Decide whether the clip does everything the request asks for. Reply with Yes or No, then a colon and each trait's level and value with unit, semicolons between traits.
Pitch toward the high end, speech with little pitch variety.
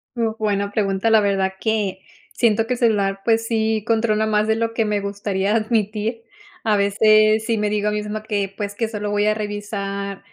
Yes: high, 210 Hz; narrow, 1.6 semitones